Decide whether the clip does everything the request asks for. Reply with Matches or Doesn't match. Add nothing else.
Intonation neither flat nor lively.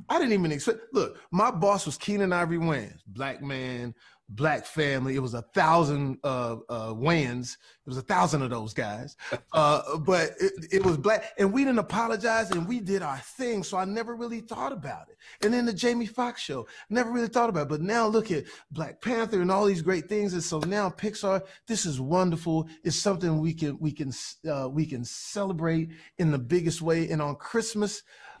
Doesn't match